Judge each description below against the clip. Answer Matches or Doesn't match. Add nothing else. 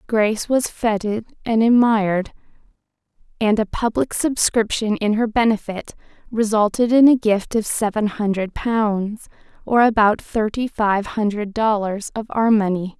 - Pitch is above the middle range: Matches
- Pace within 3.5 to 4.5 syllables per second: Matches